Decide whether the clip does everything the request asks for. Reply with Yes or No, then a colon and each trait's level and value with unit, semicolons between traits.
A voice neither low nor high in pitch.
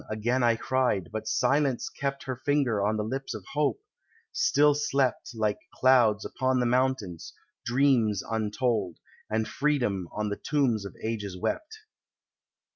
No: low, 120 Hz